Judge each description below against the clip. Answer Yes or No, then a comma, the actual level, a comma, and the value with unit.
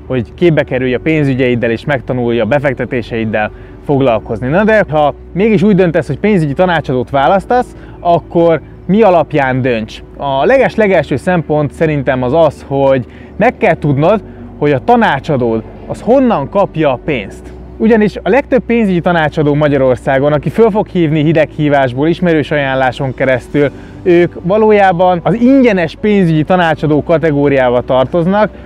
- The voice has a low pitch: No, medium, 150 Hz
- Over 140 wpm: No, average, 135 wpm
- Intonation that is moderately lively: No, wide, 5.8 semitones